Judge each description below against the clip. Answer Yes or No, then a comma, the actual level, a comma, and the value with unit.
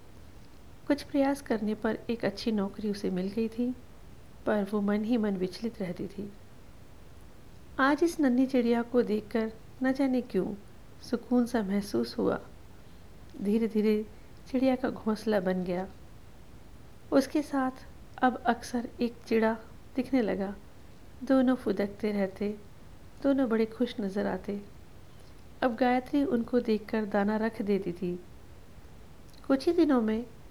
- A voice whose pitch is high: Yes, high, 225 Hz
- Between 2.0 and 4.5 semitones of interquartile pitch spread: Yes, average, 3.9 semitones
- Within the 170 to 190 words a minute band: No, average, 130 wpm